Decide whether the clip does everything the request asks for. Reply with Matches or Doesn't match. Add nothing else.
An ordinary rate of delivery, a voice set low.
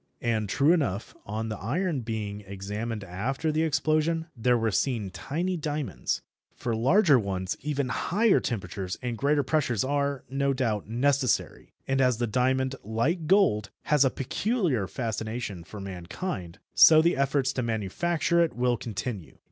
Matches